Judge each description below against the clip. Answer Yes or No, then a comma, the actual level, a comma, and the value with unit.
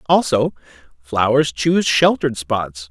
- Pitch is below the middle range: Yes, low, 125 Hz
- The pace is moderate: No, slow, 105 wpm